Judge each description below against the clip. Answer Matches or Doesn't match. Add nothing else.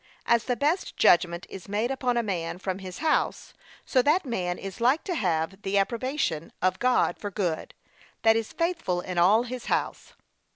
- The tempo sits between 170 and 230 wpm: Matches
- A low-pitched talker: Doesn't match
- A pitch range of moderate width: Doesn't match